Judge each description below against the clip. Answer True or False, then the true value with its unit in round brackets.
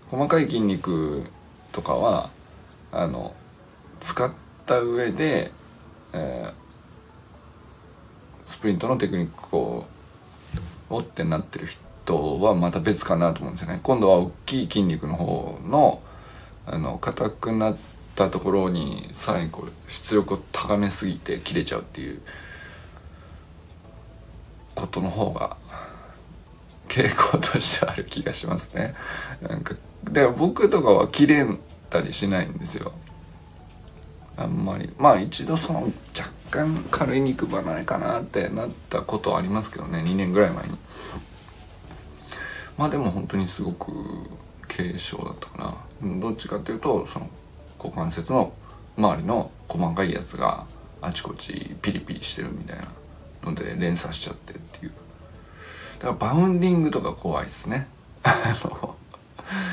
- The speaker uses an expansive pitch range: False (4.9 semitones)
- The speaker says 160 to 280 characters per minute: True (260 characters per minute)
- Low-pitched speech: True (95 Hz)